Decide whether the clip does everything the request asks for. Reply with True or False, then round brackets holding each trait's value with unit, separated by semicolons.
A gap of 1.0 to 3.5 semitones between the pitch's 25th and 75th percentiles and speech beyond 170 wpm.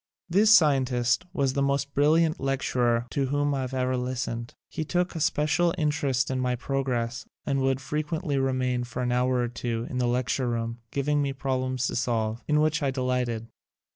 True (2.7 semitones; 180 wpm)